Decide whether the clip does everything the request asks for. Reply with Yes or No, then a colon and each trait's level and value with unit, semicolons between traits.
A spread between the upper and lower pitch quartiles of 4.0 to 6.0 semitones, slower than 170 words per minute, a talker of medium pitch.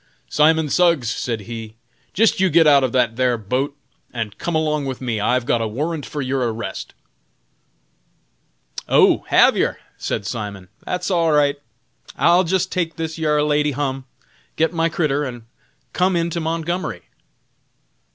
Yes: average, 5.2 semitones; average, 155 wpm; medium, 145 Hz